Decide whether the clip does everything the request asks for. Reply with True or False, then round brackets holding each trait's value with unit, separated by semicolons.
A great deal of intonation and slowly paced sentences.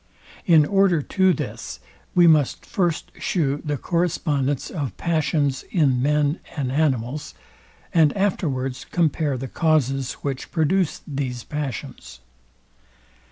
False (3.7 semitones; 115 wpm)